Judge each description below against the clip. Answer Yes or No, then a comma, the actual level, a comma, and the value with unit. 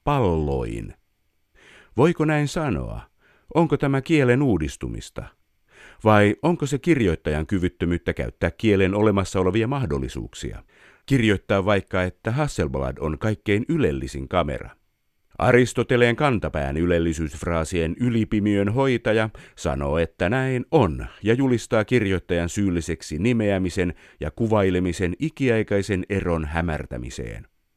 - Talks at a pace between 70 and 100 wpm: Yes, slow, 95 wpm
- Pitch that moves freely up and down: Yes, wide, 6.3 semitones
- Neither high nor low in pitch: No, low, 100 Hz